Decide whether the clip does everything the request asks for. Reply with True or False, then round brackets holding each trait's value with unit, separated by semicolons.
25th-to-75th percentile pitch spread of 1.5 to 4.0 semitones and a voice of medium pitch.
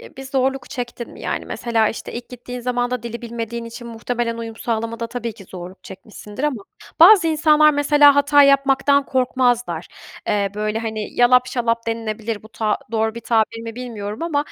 False (2.8 semitones; 235 Hz)